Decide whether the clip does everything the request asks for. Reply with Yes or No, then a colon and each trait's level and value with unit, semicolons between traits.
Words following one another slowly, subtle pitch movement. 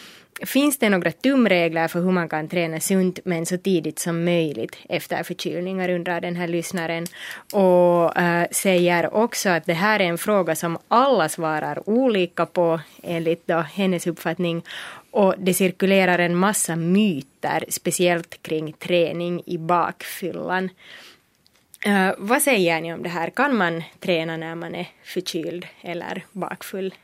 No: average, 150 wpm; narrow, 2.1 semitones